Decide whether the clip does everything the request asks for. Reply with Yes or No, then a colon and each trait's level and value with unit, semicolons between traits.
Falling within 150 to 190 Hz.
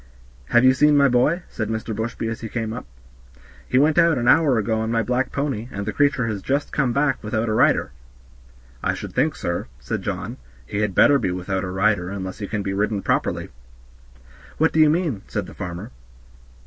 No: low, 115 Hz